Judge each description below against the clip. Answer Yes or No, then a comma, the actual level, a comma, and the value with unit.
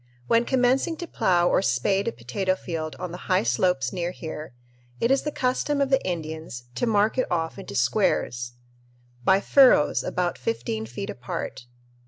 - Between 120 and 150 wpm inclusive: No, average, 170 wpm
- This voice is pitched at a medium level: Yes, medium, 180 Hz